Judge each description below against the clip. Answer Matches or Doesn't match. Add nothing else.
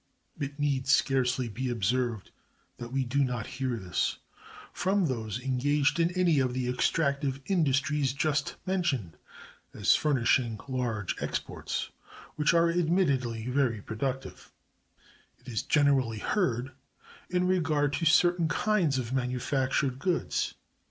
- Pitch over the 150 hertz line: Doesn't match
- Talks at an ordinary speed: Doesn't match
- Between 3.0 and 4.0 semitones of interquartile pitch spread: Matches